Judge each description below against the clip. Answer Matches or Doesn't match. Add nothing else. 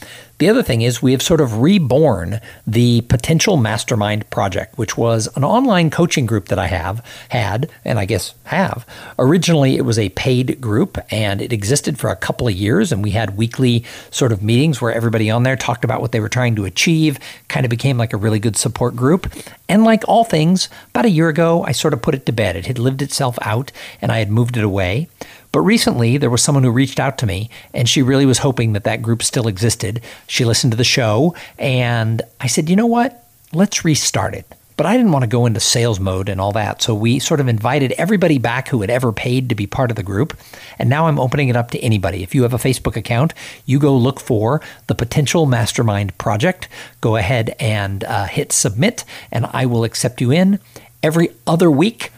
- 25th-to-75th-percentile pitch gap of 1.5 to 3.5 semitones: Doesn't match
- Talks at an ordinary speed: Doesn't match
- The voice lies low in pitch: Matches